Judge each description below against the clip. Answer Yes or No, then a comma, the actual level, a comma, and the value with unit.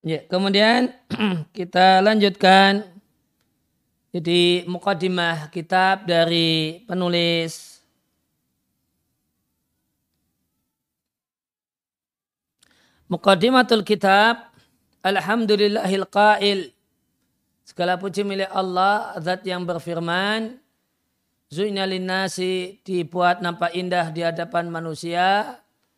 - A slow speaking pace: Yes, slow, 60 wpm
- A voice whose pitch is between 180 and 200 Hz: Yes, medium, 185 Hz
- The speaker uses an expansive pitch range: No, average, 2.7 semitones